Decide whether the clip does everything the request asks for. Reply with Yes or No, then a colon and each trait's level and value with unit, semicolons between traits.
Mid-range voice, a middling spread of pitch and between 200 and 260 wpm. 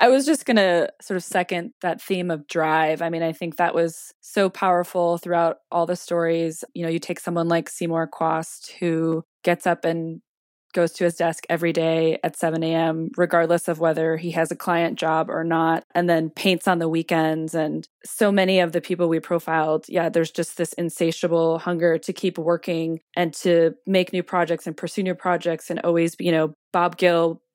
No: medium, 170 Hz; narrow, 1.4 semitones; fast, 205 wpm